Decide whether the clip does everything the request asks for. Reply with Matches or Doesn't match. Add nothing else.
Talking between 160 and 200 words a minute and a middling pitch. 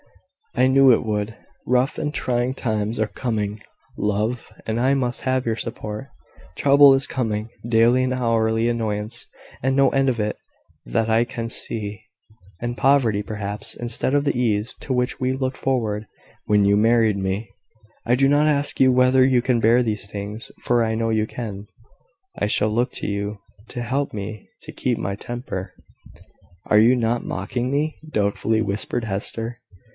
Doesn't match